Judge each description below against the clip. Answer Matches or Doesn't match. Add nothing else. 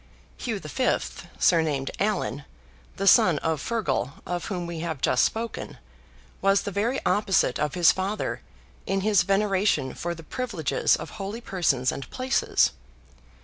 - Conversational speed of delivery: Matches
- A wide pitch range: Doesn't match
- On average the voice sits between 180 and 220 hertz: Matches